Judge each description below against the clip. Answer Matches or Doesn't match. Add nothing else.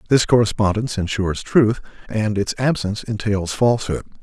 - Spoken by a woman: Doesn't match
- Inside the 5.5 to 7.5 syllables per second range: Matches